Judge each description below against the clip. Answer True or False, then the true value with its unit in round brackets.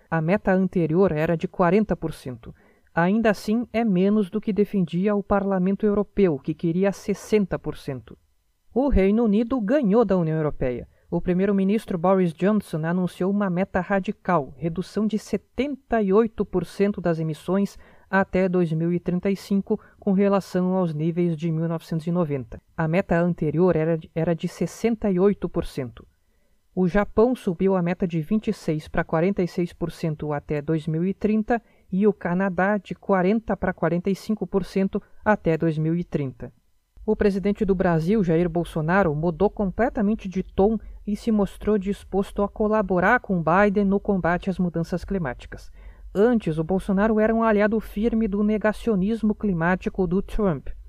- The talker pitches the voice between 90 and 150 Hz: False (190 Hz)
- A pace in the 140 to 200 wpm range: False (130 wpm)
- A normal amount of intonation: True (3.5 semitones)